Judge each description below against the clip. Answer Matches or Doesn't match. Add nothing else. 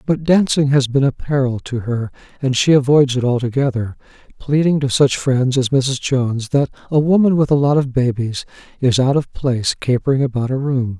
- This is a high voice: Doesn't match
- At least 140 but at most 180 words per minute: Doesn't match